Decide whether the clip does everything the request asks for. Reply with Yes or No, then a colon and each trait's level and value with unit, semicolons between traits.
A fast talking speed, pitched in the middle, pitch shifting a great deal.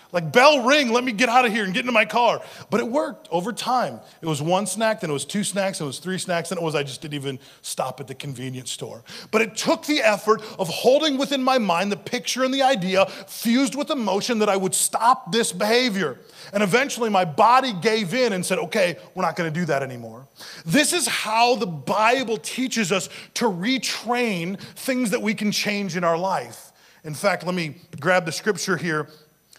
No: fast, 220 wpm; high, 205 Hz; wide, 6.1 semitones